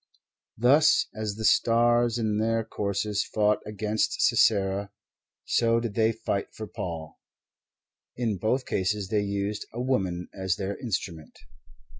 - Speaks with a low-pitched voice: Yes, low, 105 Hz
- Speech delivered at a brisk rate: No, slow, 135 wpm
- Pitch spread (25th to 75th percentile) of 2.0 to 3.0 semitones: Yes, narrow, 2.5 semitones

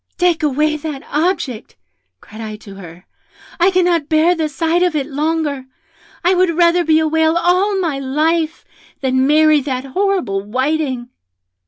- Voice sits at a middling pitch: No, very high, 310 Hz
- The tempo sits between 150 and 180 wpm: Yes, average, 155 wpm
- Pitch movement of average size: Yes, average, 4.1 semitones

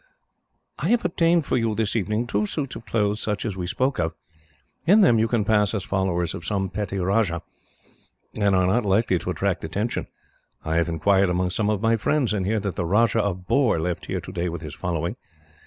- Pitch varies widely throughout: No, average, 3.9 semitones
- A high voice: No, low, 100 Hz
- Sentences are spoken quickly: Yes, fast, 210 wpm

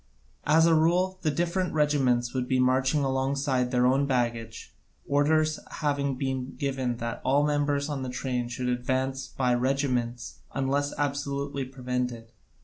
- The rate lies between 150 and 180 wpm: No, average, 140 wpm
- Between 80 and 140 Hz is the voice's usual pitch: Yes, low, 135 Hz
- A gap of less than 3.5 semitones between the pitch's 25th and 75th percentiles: Yes, narrow, 2.4 semitones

